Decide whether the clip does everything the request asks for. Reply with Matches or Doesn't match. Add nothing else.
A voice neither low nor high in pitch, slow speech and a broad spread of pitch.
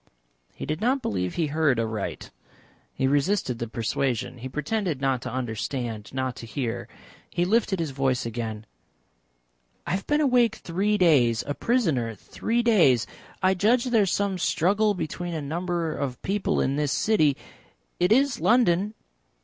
Doesn't match